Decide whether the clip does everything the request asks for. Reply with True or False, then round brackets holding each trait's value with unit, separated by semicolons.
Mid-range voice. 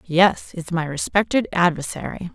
True (175 Hz)